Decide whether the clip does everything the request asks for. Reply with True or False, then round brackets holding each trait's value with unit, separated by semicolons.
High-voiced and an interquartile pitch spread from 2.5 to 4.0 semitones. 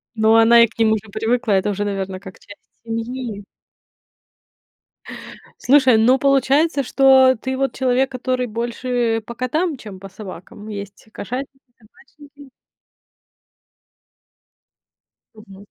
True (235 Hz; 3.7 semitones)